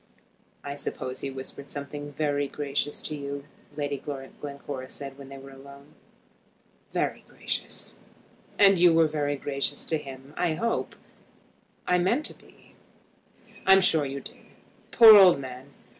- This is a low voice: No, medium, 145 Hz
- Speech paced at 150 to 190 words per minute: No, average, 140 wpm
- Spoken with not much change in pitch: Yes, narrow, 2.2 semitones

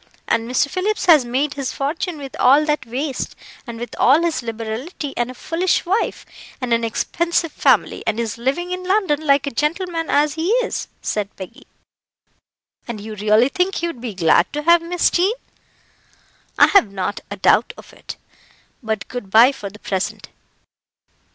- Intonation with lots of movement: Yes, wide, 6.6 semitones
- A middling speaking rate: Yes, average, 175 wpm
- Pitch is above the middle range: Yes, very high, 275 Hz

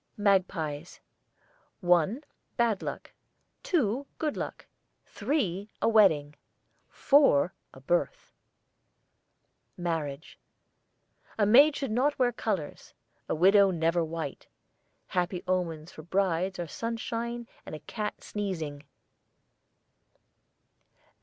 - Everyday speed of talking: No, slow, 95 wpm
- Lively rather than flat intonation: Yes, wide, 5.8 semitones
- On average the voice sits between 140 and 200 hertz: Yes, high, 190 Hz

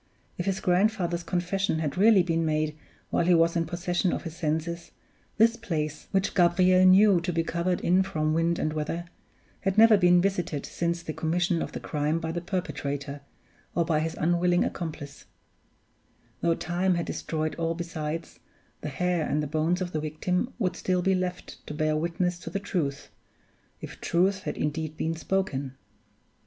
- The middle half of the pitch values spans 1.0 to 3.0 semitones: Yes, narrow, 2.6 semitones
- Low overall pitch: No, medium, 170 Hz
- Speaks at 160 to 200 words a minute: Yes, average, 175 wpm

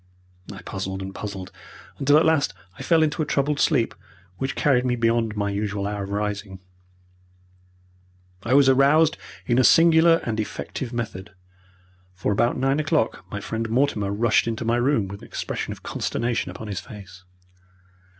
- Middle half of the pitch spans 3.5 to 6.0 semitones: Yes, average, 5.3 semitones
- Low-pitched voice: Yes, low, 115 Hz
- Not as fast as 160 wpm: No, average, 165 wpm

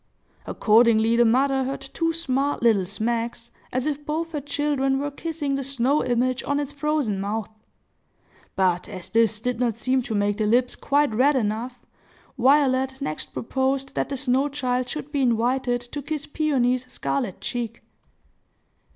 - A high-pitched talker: Yes, very high, 255 Hz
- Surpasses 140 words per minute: Yes, average, 160 wpm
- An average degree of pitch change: Yes, average, 3.4 semitones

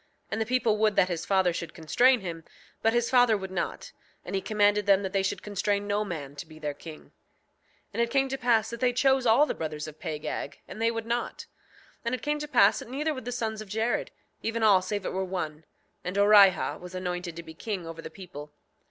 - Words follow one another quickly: Yes, fast, 240 wpm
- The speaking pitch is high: Yes, high, 205 Hz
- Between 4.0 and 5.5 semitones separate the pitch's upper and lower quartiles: Yes, average, 4.7 semitones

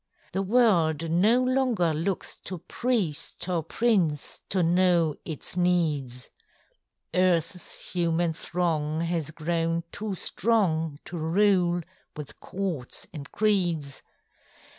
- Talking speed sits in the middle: No, slow, 105 wpm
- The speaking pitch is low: No, medium, 175 Hz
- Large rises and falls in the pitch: No, average, 3.2 semitones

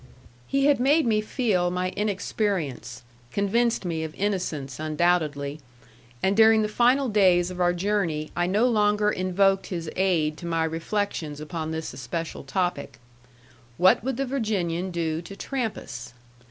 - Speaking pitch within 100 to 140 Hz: No, medium, 185 Hz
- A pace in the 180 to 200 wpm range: No, average, 145 wpm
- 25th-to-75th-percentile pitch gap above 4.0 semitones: Yes, average, 4.6 semitones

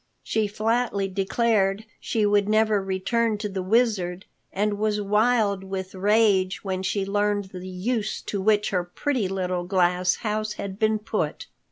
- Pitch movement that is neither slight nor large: No, narrow, 2.2 semitones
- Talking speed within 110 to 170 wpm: Yes, average, 155 wpm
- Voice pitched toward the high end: Yes, high, 205 Hz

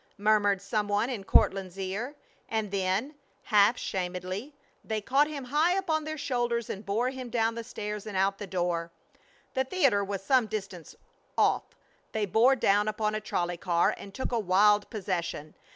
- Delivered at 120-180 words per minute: Yes, average, 170 wpm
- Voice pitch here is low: No, high, 210 Hz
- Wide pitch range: No, average, 3.9 semitones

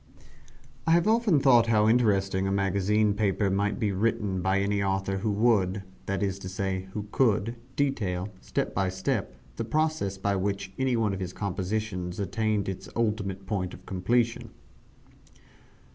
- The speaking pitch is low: Yes, low, 100 Hz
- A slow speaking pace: No, average, 160 wpm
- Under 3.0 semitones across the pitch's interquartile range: Yes, narrow, 2.6 semitones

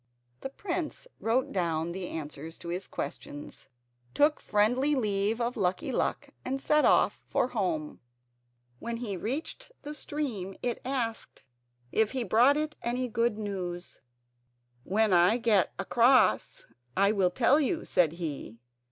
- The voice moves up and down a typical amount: No, wide, 6.2 semitones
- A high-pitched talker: Yes, high, 220 Hz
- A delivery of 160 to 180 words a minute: No, average, 145 wpm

